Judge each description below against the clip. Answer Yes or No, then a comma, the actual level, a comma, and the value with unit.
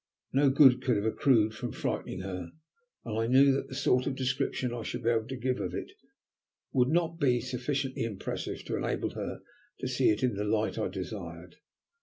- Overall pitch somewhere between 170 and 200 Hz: No, low, 125 Hz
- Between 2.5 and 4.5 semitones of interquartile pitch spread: Yes, average, 3.1 semitones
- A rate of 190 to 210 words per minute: Yes, average, 200 wpm